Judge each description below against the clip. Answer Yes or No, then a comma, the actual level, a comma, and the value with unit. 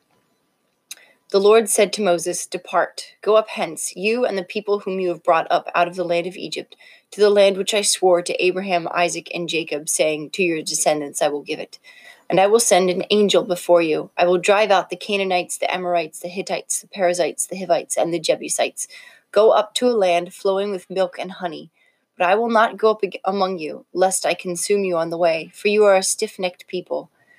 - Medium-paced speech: No, fast, 220 wpm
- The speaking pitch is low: No, medium, 185 Hz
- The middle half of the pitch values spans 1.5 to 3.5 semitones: Yes, average, 2.9 semitones